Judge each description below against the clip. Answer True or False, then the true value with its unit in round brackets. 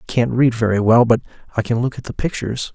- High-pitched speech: False (120 Hz)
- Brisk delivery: True (260 wpm)